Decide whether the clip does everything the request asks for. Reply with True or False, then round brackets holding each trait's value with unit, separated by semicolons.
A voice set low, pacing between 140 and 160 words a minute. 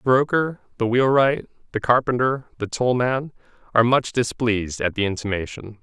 True (120 Hz; 155 wpm)